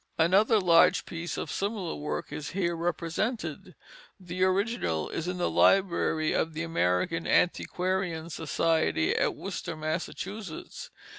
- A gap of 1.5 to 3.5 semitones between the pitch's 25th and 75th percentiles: Yes, average, 2.8 semitones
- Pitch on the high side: No, medium, 170 Hz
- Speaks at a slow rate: Yes, slow, 125 wpm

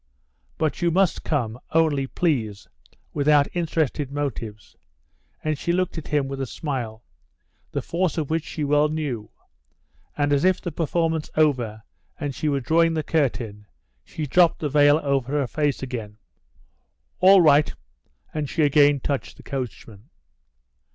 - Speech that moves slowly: No, average, 150 wpm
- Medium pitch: Yes, medium, 145 Hz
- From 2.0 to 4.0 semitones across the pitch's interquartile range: Yes, average, 3.3 semitones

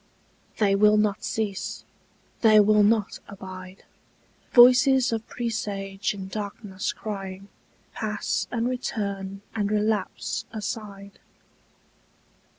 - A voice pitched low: No, high, 210 Hz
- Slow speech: Yes, slow, 95 wpm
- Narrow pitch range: Yes, narrow, 2.0 semitones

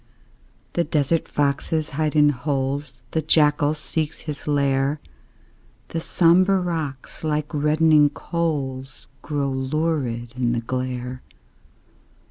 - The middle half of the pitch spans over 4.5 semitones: No, average, 2.9 semitones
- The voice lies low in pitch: No, medium, 145 Hz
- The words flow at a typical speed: No, slow, 105 wpm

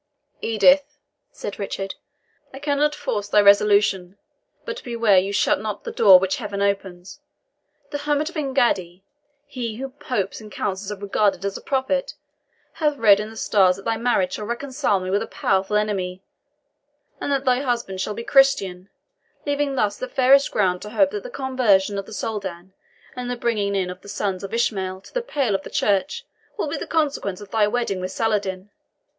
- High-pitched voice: Yes, high, 210 Hz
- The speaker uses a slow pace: No, average, 185 wpm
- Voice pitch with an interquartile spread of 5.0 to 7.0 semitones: Yes, average, 5.3 semitones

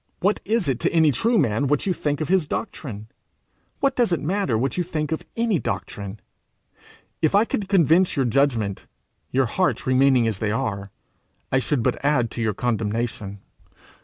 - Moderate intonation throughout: No, wide, 7.6 semitones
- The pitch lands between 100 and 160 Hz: Yes, medium, 140 Hz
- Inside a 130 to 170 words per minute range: No, average, 180 wpm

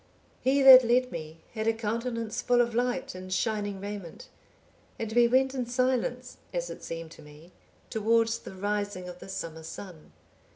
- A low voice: No, high, 220 Hz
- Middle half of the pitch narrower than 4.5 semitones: No, average, 4.9 semitones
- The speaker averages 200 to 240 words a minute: No, average, 175 wpm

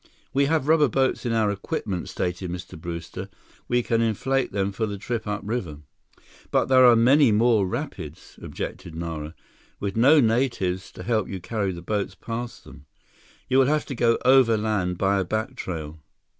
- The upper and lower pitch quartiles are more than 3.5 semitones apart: Yes, average, 5.0 semitones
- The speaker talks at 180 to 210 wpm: No, average, 170 wpm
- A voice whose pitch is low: Yes, low, 110 Hz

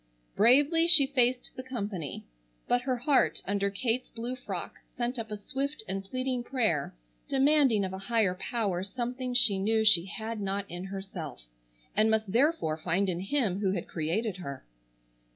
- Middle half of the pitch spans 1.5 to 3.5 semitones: No, average, 4.7 semitones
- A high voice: Yes, high, 220 Hz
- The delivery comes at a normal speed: Yes, average, 165 wpm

